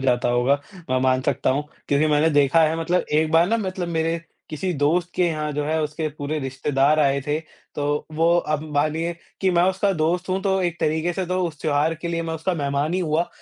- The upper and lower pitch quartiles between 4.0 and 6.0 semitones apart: No, average, 2.9 semitones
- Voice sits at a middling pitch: Yes, medium, 155 Hz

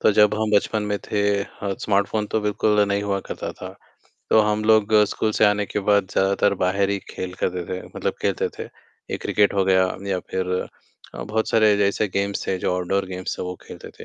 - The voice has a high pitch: No, low, 100 Hz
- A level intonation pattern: Yes, narrow, 1.6 semitones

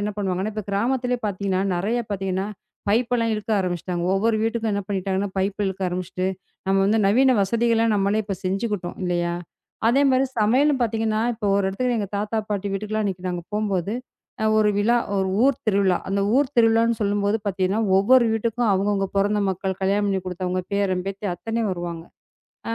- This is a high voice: Yes, high, 205 Hz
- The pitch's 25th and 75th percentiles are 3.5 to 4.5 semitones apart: No, average, 2.8 semitones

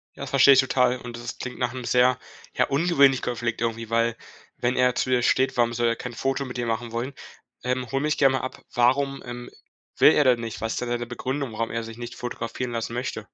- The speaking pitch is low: Yes, low, 125 Hz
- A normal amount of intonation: No, narrow, 1.8 semitones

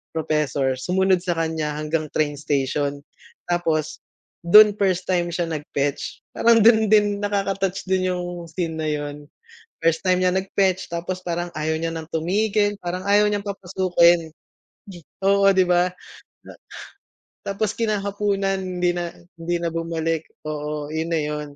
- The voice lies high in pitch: No, medium, 175 Hz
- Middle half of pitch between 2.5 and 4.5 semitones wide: Yes, average, 3.5 semitones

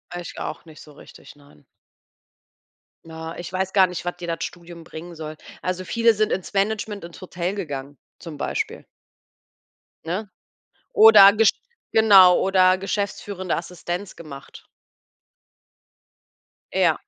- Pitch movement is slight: No, average, 3.2 semitones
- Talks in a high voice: No, medium, 180 Hz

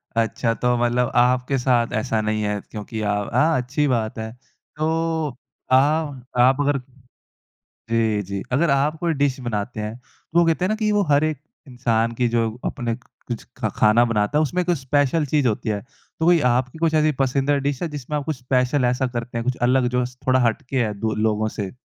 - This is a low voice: Yes, low, 125 Hz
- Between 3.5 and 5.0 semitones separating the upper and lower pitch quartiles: Yes, average, 4.0 semitones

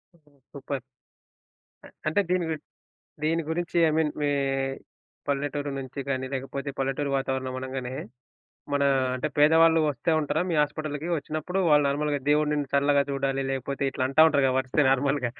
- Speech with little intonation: Yes, narrow, 2.2 semitones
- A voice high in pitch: No, medium, 145 Hz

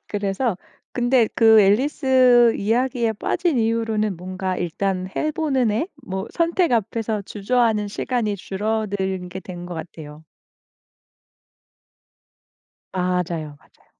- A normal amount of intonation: Yes, average, 4.5 semitones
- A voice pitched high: Yes, high, 210 Hz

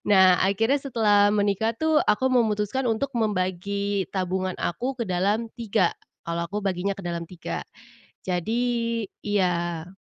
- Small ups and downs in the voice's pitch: No, average, 3.5 semitones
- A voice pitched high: Yes, high, 200 Hz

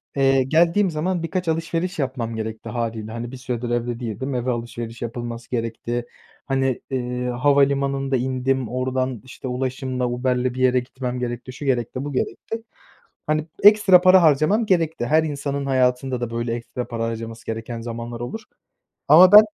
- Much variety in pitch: No, average, 3.0 semitones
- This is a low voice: Yes, low, 130 Hz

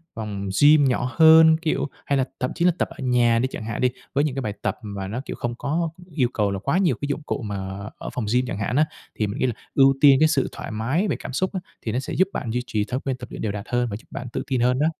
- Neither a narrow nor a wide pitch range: Yes, average, 4.8 semitones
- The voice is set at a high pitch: No, low, 125 Hz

